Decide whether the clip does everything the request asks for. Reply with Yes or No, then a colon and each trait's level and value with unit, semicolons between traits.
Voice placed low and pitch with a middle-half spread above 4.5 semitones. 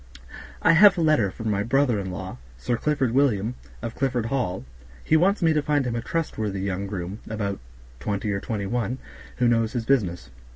Yes: low, 115 Hz; wide, 5.5 semitones